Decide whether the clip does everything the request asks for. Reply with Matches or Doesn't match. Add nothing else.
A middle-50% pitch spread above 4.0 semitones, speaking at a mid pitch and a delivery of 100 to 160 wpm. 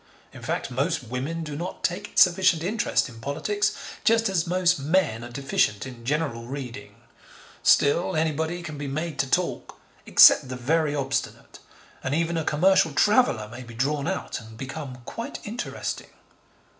Matches